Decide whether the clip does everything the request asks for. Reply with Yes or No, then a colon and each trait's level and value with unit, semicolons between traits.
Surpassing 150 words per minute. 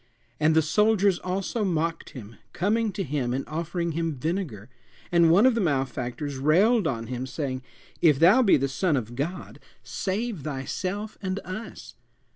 Yes: average, 160 wpm